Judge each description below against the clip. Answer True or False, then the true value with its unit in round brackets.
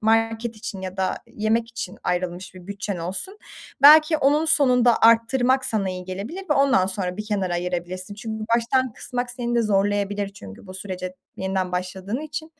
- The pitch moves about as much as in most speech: True (4.7 semitones)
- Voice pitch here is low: False (210 Hz)